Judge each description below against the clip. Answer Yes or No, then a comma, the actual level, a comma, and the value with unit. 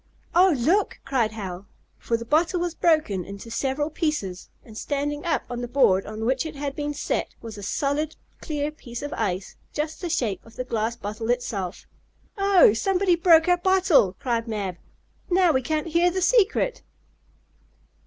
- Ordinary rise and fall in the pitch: No, wide, 6.9 semitones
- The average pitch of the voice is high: Yes, very high, 280 Hz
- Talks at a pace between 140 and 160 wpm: No, average, 175 wpm